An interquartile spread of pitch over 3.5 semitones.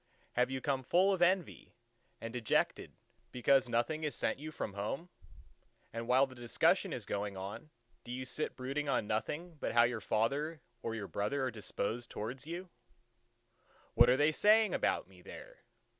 Yes: average, 4.7 semitones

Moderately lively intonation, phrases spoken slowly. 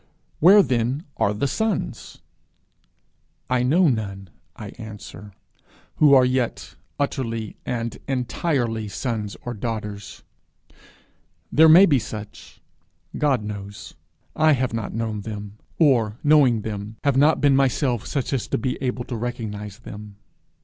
Yes: average, 4.3 semitones; slow, 130 wpm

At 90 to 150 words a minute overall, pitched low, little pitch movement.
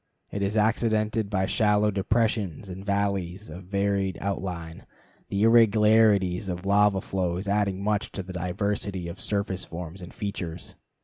Yes: average, 140 wpm; low, 100 Hz; narrow, 2.1 semitones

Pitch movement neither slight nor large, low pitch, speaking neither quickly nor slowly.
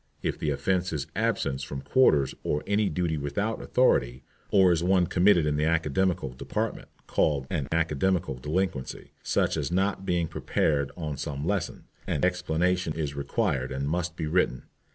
Yes: average, 4.4 semitones; very low, 80 Hz; average, 160 wpm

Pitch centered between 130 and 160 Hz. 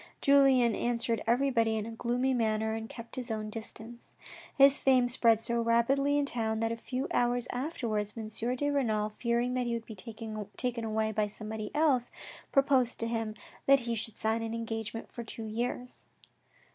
No: high, 230 Hz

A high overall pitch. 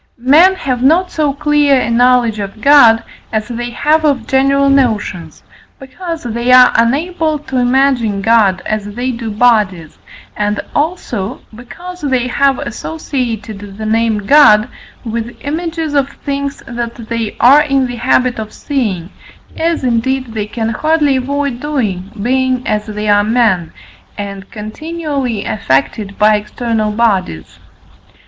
Yes: high, 245 Hz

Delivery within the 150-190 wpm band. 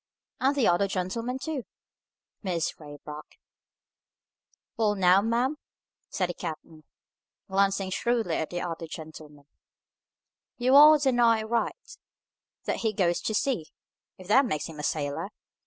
No: average, 140 wpm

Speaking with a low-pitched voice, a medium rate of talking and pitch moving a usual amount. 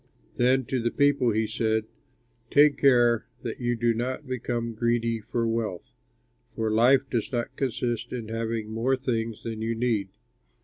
No: low, 115 Hz; average, 160 wpm; narrow, 1.9 semitones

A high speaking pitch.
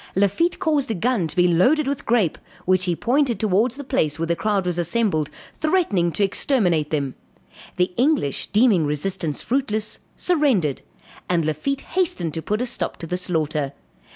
Yes: high, 195 Hz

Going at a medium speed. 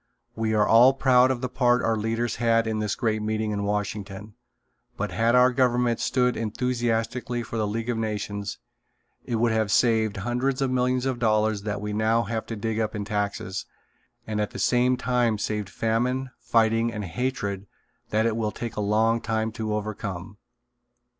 Yes: average, 180 wpm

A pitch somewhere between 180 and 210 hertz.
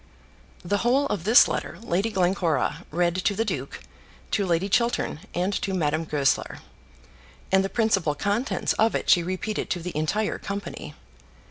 Yes: high, 190 Hz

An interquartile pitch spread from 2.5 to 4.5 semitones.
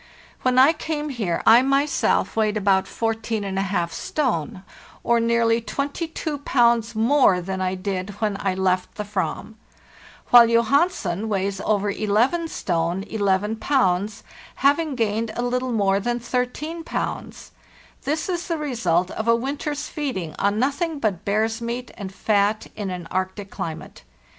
No: average, 4.9 semitones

